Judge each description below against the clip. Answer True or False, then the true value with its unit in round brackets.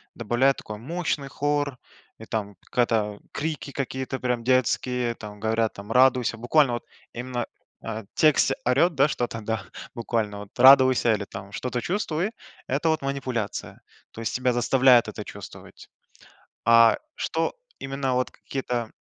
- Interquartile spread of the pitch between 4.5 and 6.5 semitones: False (3.2 semitones)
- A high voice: False (125 Hz)